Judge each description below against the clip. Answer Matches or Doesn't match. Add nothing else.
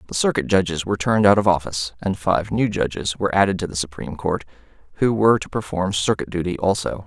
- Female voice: Doesn't match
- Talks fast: Matches